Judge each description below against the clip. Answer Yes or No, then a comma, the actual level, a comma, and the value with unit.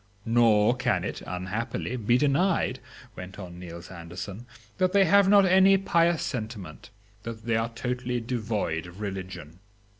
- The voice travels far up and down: Yes, wide, 6.0 semitones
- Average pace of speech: Yes, average, 145 wpm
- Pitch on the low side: Yes, low, 115 Hz